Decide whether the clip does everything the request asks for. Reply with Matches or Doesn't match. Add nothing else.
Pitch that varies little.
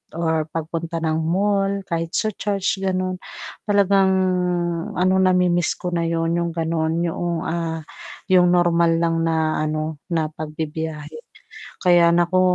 Matches